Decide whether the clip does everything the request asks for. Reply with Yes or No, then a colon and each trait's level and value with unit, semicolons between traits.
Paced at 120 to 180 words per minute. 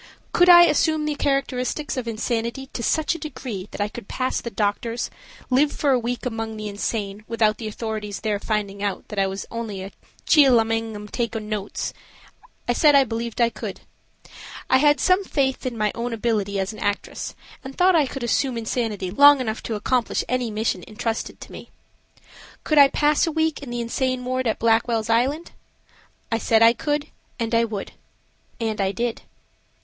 No: average, 190 wpm